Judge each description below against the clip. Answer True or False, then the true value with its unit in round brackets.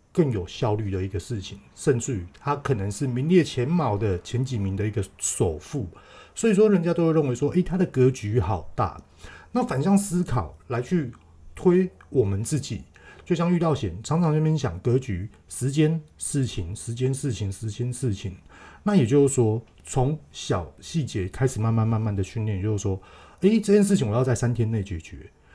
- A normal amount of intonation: False (7.4 semitones)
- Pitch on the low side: True (120 Hz)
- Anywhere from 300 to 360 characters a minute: False (275 characters per minute)